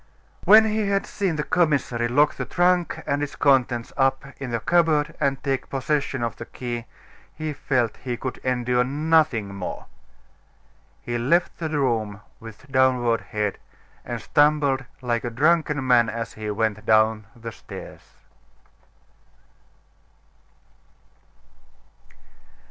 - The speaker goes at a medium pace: No, slow, 125 wpm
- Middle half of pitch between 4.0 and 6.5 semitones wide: Yes, average, 4.3 semitones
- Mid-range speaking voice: No, low, 130 Hz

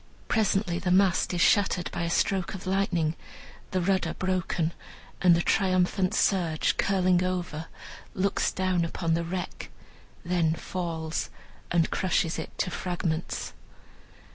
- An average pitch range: No, narrow, 1.8 semitones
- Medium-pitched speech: Yes, medium, 180 Hz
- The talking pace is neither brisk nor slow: No, slow, 130 wpm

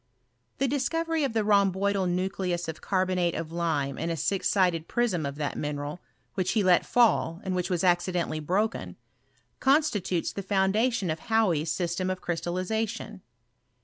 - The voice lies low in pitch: No, medium, 185 Hz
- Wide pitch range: No, average, 3.9 semitones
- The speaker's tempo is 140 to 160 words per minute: Yes, average, 155 wpm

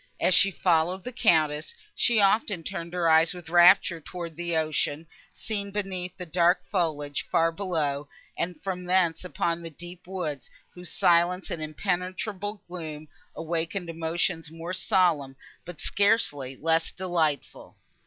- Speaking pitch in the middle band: Yes, medium, 175 Hz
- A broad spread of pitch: No, narrow, 2.4 semitones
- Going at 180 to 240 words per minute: No, average, 140 wpm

